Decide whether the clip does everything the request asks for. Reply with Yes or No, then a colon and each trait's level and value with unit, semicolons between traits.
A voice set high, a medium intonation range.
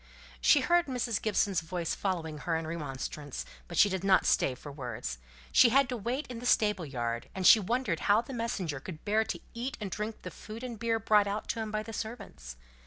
No: high, 205 Hz; wide, 6.2 semitones